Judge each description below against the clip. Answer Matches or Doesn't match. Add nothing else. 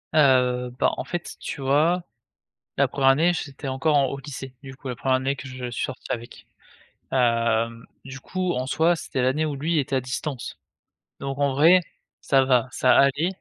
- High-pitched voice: Doesn't match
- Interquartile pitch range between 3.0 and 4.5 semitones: Doesn't match